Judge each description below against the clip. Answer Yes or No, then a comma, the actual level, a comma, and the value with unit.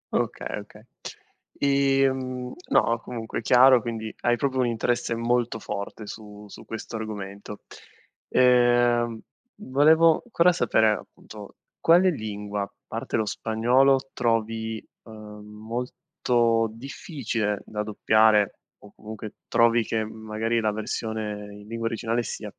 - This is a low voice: Yes, low, 115 Hz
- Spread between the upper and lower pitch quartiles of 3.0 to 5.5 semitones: No, narrow, 2.5 semitones